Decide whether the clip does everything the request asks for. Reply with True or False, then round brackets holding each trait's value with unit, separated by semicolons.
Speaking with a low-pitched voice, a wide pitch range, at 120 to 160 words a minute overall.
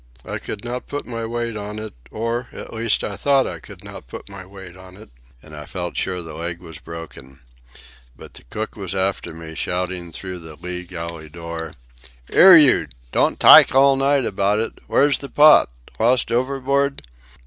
False (100 Hz; 6.2 semitones; 185 wpm)